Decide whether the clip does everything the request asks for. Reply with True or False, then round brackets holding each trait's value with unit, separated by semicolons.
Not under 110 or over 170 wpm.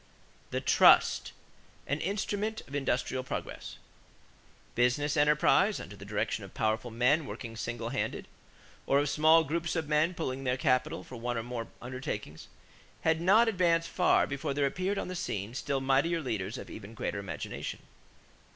True (160 wpm)